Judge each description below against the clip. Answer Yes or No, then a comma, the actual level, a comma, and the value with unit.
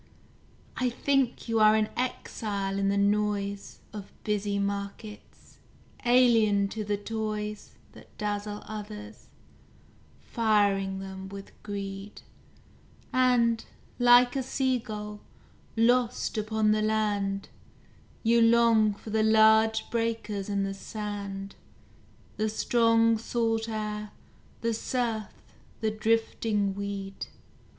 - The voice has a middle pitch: No, high, 215 Hz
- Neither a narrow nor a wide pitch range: No, narrow, 2.1 semitones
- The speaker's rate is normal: No, slow, 105 wpm